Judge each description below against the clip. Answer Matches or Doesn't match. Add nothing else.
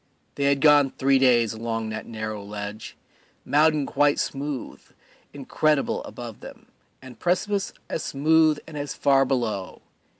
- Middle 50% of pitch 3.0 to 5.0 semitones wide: Matches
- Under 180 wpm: Matches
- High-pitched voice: Doesn't match